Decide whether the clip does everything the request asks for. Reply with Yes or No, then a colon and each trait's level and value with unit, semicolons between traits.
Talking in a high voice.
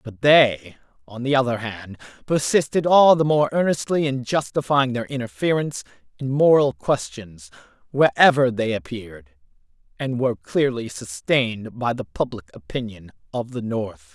No: low, 130 Hz